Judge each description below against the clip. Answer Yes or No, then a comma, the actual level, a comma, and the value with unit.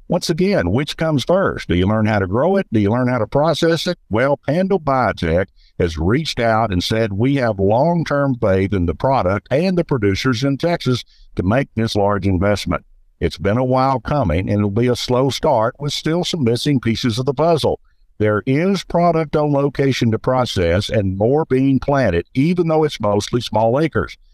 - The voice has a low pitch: Yes, low, 130 Hz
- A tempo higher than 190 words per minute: Yes, average, 200 wpm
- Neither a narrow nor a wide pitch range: No, wide, 5.8 semitones